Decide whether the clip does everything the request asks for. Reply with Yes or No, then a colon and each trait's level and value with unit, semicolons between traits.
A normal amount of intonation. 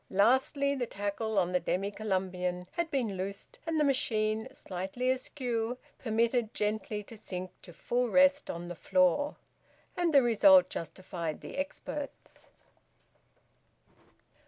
No: wide, 5.9 semitones